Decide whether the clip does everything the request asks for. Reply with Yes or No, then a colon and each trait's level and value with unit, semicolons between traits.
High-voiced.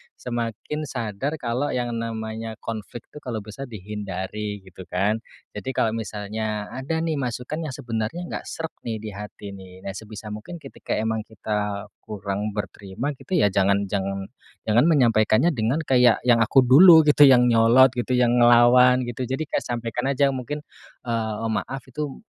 No: low, 115 Hz